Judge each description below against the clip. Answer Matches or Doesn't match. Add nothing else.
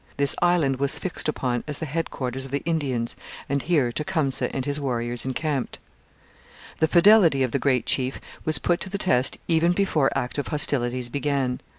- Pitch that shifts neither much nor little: Matches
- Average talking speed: Matches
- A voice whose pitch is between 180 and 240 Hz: Doesn't match